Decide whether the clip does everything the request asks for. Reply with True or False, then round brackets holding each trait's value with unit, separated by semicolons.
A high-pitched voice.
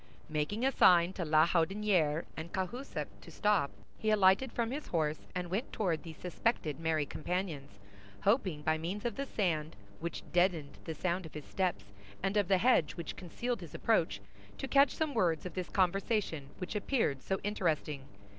False (180 Hz)